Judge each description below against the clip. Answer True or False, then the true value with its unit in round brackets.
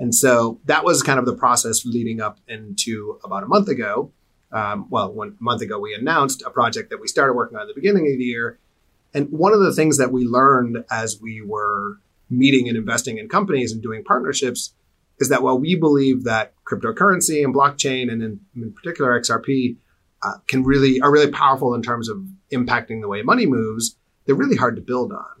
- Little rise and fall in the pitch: False (3.7 semitones)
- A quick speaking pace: True (210 wpm)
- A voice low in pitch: True (125 Hz)